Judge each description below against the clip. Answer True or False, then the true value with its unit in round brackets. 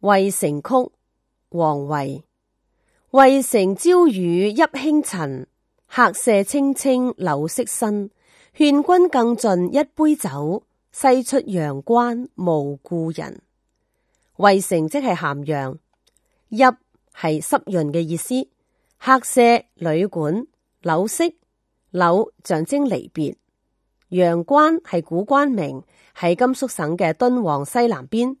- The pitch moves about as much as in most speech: False (7.8 semitones)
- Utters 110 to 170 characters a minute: True (155 characters per minute)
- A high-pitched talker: True (200 Hz)